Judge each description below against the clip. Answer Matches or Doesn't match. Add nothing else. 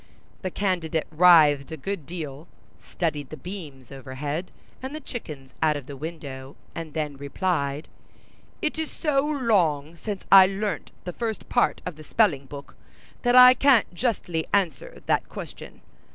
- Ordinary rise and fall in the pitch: Doesn't match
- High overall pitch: Doesn't match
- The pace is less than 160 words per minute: Matches